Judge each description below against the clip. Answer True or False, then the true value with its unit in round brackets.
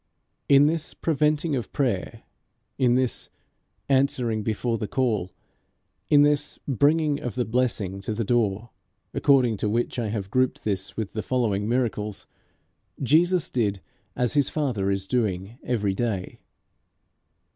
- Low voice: True (120 Hz)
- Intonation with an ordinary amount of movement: True (4.7 semitones)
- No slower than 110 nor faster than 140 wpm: True (135 wpm)